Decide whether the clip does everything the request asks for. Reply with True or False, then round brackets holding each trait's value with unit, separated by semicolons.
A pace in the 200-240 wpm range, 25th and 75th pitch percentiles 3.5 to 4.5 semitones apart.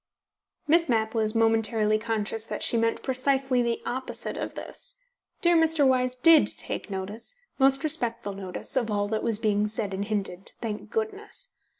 False (165 wpm; 4.0 semitones)